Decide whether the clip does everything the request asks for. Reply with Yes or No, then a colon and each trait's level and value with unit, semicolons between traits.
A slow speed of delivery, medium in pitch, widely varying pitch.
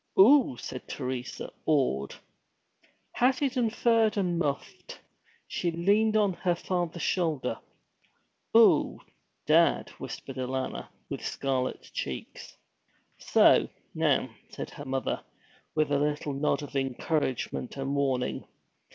Yes: slow, 110 wpm; medium, 150 Hz; wide, 5.8 semitones